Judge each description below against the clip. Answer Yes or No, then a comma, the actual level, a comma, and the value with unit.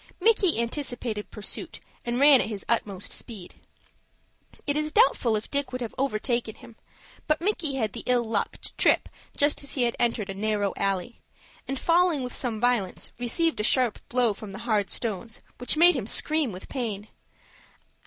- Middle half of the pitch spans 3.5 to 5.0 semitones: Yes, average, 4.6 semitones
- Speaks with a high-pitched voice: Yes, high, 240 Hz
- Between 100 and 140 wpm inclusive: No, average, 175 wpm